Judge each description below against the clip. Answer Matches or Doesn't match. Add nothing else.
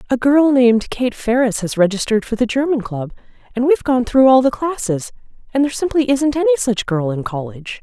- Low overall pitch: Doesn't match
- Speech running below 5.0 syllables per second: Doesn't match